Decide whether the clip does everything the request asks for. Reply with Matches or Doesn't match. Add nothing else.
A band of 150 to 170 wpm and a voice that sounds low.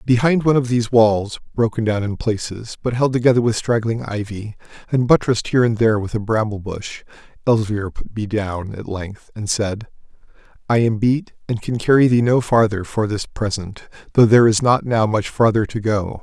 Doesn't match